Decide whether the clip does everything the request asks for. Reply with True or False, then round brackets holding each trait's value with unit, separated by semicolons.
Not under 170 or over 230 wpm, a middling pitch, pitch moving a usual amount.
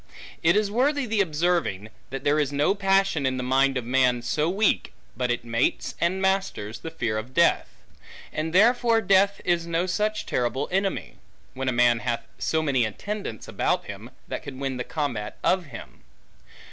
False (180 wpm; 155 Hz; 7.4 semitones)